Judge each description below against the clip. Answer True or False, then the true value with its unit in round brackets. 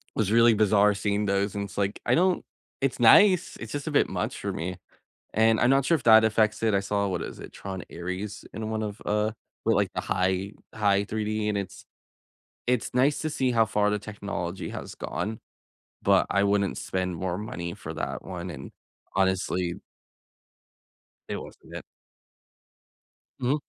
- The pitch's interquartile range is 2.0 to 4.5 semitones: True (2.6 semitones)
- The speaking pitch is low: True (105 Hz)